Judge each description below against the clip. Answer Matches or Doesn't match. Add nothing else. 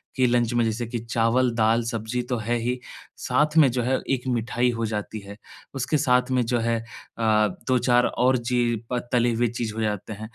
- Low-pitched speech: Matches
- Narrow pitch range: Matches